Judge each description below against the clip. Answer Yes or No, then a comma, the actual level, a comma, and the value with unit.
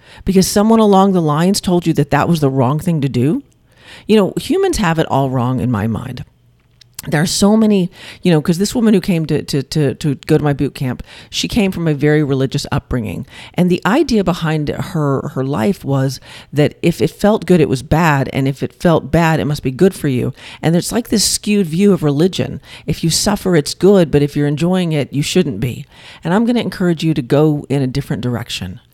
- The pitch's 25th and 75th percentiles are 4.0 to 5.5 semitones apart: Yes, average, 5.1 semitones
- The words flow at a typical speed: No, fast, 230 wpm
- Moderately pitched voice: Yes, medium, 155 Hz